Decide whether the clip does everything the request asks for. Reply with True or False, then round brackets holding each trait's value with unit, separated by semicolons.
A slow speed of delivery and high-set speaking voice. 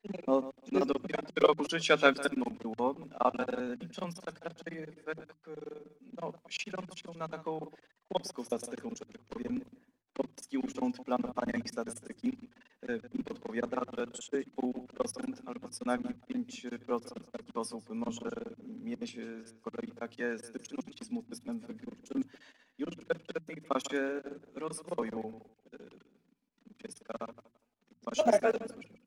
True (105 wpm; 195 Hz)